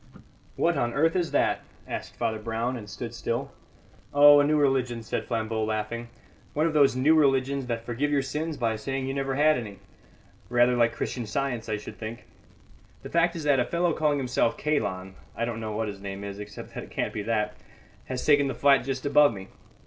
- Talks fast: Yes, fast, 210 wpm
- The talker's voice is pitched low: Yes, low, 125 Hz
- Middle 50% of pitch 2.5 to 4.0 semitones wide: No, average, 4.4 semitones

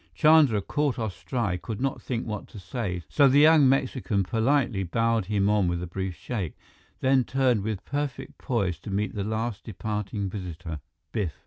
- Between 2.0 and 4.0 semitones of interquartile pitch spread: No, average, 5.2 semitones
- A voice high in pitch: No, low, 110 Hz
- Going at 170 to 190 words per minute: Yes, average, 180 wpm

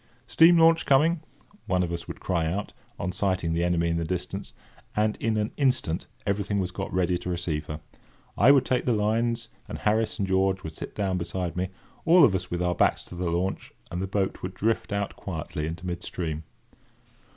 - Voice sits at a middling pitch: No, very low, 95 Hz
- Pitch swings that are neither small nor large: Yes, average, 3.7 semitones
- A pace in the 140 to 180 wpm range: No, fast, 205 wpm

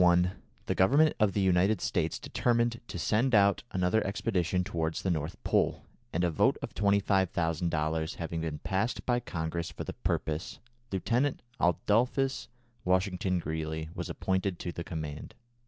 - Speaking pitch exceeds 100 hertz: No, very low, 90 Hz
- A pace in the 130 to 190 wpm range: Yes, average, 155 wpm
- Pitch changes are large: No, average, 3.7 semitones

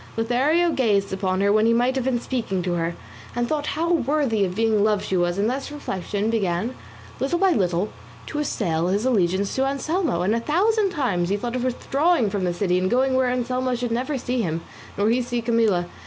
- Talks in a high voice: Yes, high, 230 Hz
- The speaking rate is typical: No, fast, 215 wpm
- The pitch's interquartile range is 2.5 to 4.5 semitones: No, average, 5.2 semitones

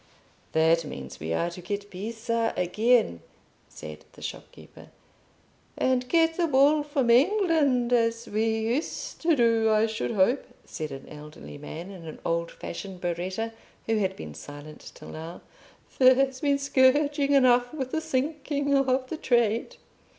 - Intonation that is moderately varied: No, wide, 7.2 semitones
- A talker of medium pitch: No, high, 230 Hz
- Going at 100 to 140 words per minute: No, average, 150 wpm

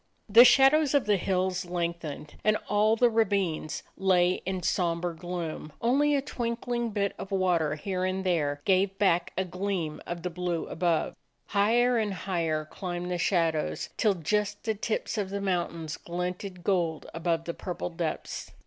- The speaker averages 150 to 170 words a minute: Yes, average, 165 wpm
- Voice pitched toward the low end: No, medium, 185 Hz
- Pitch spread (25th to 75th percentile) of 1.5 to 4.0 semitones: Yes, average, 3.2 semitones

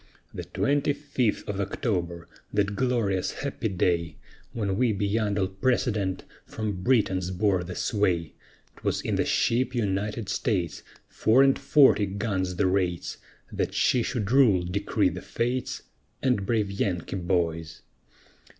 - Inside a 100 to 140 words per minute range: Yes, slow, 135 wpm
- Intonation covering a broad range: No, average, 4.2 semitones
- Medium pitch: No, low, 100 Hz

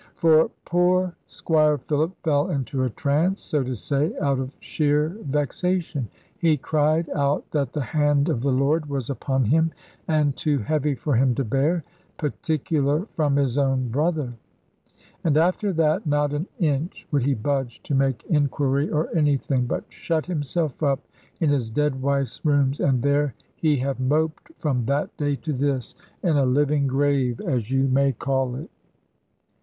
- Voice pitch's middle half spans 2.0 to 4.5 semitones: Yes, narrow, 2.5 semitones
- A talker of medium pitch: Yes, medium, 145 Hz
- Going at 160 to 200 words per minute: Yes, average, 165 wpm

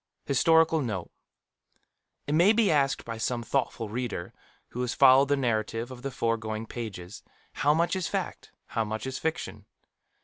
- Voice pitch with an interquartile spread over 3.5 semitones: Yes, average, 4.4 semitones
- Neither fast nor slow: Yes, average, 150 wpm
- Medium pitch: No, low, 125 Hz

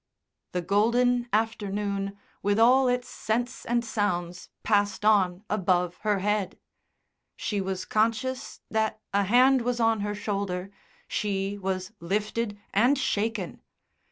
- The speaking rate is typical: No, slow, 125 wpm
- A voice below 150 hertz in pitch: No, high, 210 Hz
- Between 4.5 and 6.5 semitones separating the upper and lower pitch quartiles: No, average, 2.9 semitones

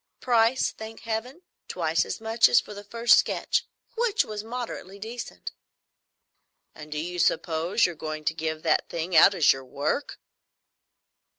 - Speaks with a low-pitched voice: No, high, 200 Hz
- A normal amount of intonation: No, wide, 6.3 semitones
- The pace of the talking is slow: No, average, 155 wpm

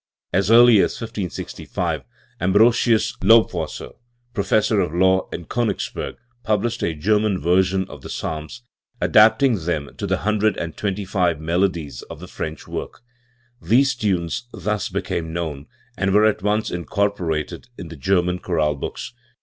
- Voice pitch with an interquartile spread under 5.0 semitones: Yes, average, 4.2 semitones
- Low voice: Yes, very low, 95 Hz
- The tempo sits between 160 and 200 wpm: No, average, 140 wpm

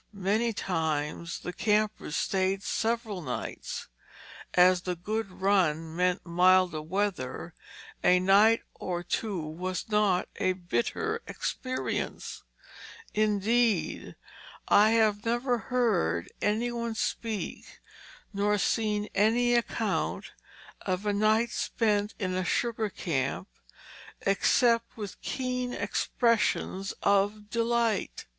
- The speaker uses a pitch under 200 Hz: No, high, 205 Hz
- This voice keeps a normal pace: No, slow, 105 wpm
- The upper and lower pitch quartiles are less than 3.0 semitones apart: No, average, 3.8 semitones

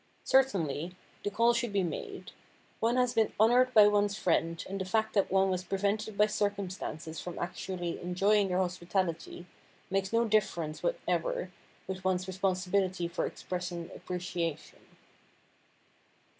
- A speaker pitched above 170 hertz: Yes, high, 190 Hz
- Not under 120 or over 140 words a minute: Yes, slow, 135 wpm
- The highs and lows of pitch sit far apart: No, average, 3.0 semitones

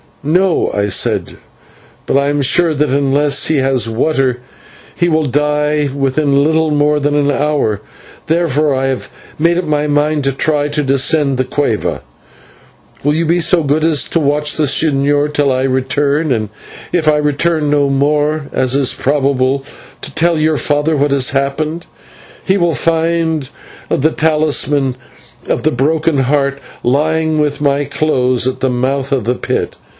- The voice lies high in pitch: No, medium, 145 Hz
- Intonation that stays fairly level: Yes, narrow, 2.3 semitones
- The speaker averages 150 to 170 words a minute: Yes, average, 165 wpm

